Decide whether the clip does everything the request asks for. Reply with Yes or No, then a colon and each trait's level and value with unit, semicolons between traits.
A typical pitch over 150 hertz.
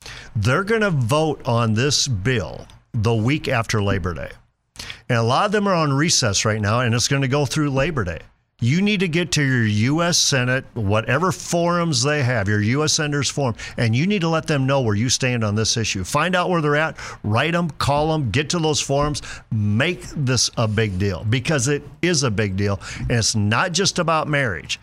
No: low, 135 Hz